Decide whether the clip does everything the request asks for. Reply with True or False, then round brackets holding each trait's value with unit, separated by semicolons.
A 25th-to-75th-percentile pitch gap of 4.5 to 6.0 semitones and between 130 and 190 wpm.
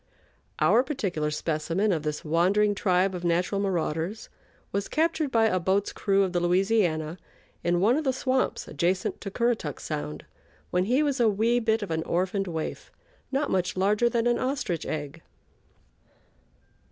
True (4.9 semitones; 160 wpm)